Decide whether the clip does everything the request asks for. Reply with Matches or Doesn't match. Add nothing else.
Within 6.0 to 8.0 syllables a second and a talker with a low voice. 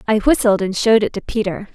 Doesn't match